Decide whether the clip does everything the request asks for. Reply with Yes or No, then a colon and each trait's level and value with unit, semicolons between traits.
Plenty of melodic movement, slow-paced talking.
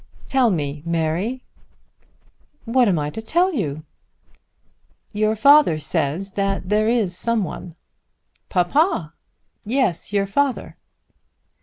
Yes: wide, 6.4 semitones; slow, 110 wpm